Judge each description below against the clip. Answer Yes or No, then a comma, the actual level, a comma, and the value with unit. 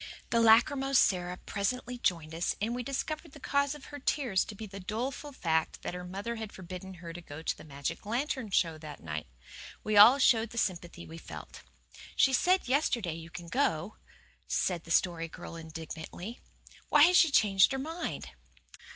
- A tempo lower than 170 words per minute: No, average, 185 wpm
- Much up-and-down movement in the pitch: Yes, wide, 7.6 semitones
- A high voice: Yes, high, 205 Hz